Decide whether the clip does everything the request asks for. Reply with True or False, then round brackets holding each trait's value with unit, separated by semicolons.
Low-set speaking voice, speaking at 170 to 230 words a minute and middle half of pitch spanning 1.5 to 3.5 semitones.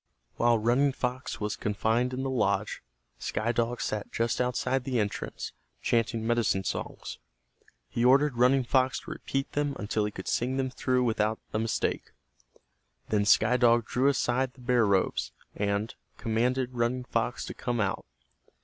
False (120 Hz; 160 wpm; 2.6 semitones)